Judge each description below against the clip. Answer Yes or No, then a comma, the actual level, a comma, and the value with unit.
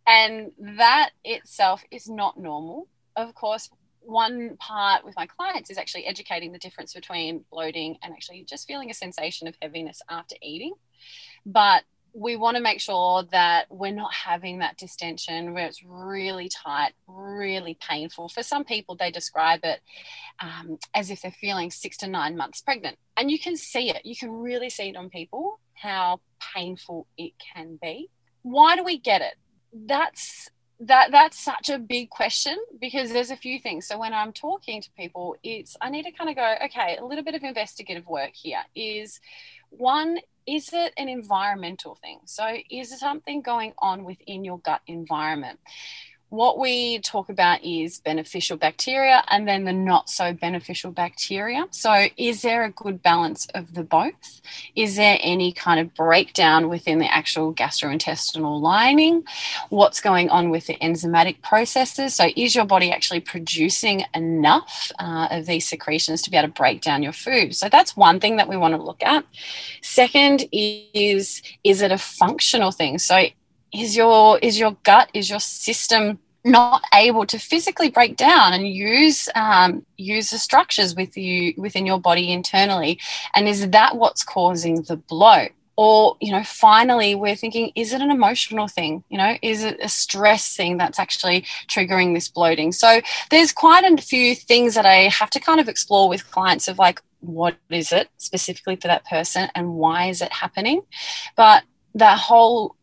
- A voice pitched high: Yes, high, 200 Hz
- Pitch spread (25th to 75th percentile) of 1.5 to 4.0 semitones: No, wide, 5.4 semitones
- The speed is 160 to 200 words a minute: Yes, average, 175 wpm